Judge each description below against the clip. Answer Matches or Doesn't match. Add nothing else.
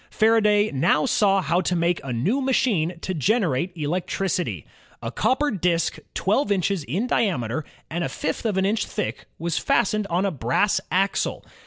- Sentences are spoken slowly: Doesn't match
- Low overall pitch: Doesn't match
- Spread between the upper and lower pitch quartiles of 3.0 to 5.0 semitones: Matches